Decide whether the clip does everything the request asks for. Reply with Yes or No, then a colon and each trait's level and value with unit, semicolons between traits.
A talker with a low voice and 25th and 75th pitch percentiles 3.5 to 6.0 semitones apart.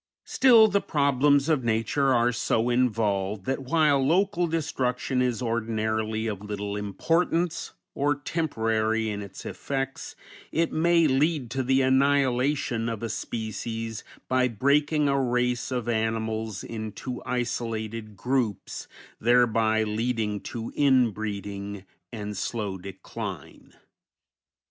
Yes: low, 120 Hz; average, 4.0 semitones